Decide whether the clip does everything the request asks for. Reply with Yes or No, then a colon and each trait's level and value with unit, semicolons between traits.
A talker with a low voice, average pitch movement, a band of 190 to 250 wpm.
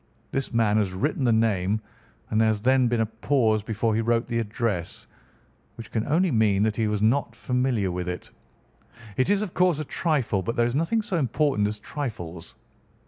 Yes: low, 115 Hz; average, 4.1 semitones; average, 195 wpm